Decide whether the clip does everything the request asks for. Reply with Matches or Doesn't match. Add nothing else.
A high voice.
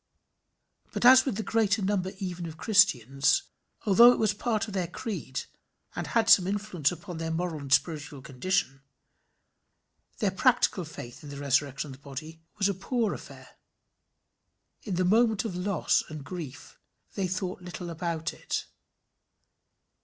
Doesn't match